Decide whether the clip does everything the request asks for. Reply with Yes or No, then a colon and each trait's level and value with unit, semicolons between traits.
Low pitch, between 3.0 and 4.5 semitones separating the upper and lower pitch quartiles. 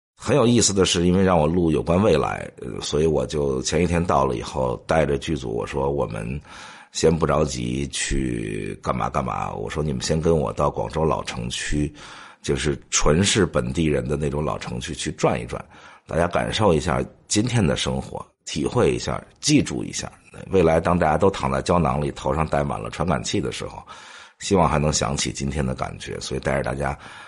Yes: very low, 75 Hz; average, 3.9 semitones